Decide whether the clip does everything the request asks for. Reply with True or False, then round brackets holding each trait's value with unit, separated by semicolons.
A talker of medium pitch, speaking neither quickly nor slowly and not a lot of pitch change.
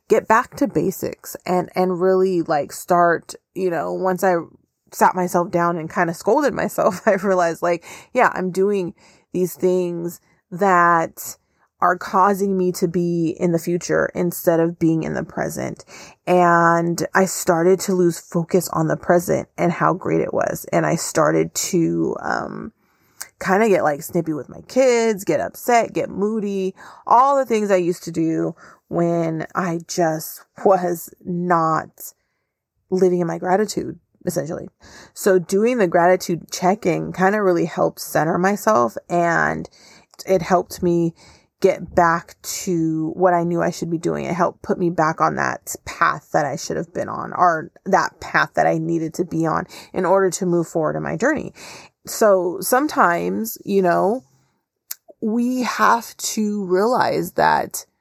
True (180 Hz; 160 wpm; 2.1 semitones)